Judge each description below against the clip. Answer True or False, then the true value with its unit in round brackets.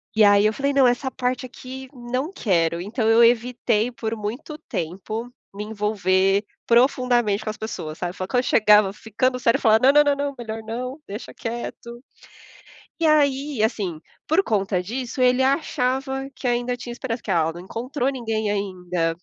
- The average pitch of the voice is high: True (235 Hz)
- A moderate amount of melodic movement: True (3.7 semitones)